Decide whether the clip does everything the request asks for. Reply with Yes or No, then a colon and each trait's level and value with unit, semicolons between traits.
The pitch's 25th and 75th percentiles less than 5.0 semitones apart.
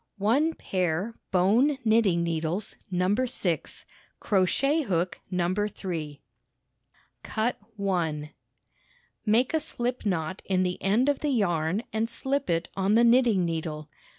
No: average, 5.3 semitones